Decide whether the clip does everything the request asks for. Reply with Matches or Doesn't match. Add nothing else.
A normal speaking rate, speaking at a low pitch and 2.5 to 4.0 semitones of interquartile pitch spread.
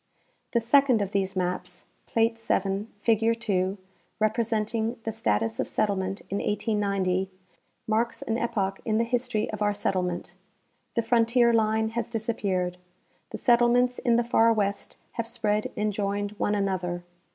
Doesn't match